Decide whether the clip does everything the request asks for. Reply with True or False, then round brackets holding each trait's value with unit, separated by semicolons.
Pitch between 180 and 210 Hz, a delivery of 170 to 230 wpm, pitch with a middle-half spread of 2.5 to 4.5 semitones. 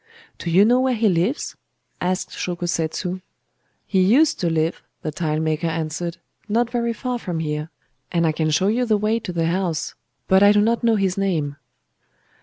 False (185 Hz; 185 wpm; 5.0 semitones)